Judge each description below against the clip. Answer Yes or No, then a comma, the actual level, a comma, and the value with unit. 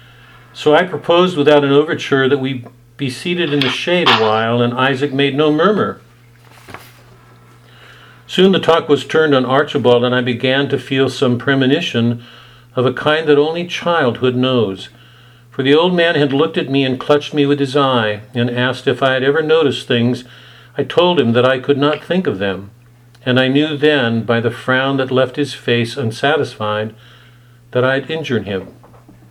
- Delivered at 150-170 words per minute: No, average, 185 wpm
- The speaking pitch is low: Yes, low, 130 Hz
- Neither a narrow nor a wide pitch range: Yes, average, 3.4 semitones